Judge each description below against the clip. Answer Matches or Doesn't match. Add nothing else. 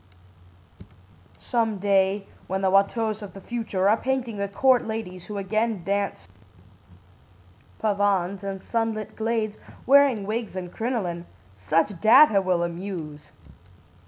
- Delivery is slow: Matches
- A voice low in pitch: Doesn't match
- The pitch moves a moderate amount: Matches